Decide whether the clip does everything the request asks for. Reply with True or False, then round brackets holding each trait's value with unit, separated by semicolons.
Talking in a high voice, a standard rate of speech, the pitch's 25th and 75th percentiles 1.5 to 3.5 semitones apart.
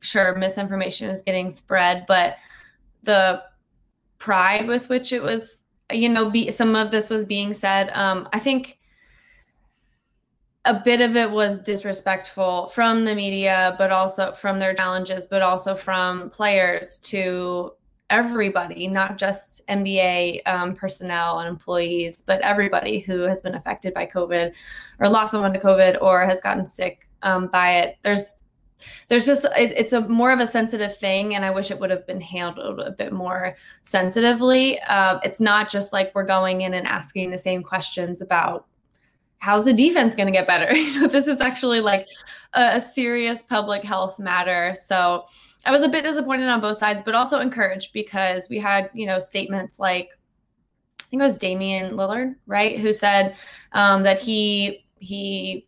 True (195 Hz; 170 wpm; 3.0 semitones)